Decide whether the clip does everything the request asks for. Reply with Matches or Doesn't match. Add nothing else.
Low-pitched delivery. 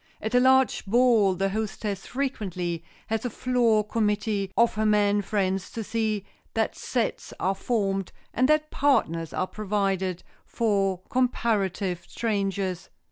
Doesn't match